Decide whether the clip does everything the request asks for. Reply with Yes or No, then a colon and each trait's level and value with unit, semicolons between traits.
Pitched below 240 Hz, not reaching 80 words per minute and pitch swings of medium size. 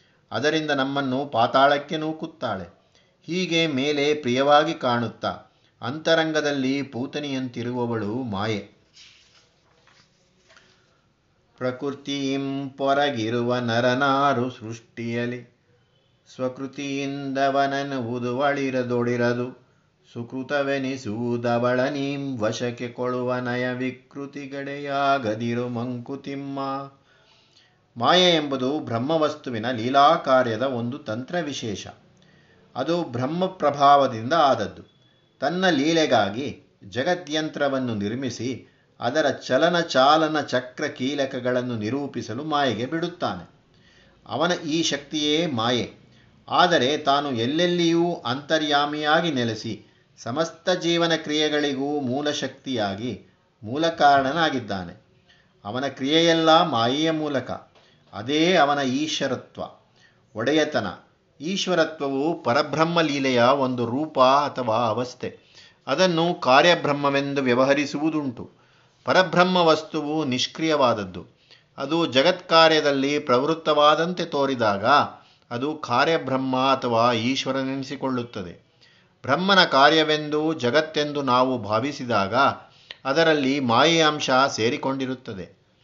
Yes: medium, 140 Hz; average, 70 wpm; average, 3.7 semitones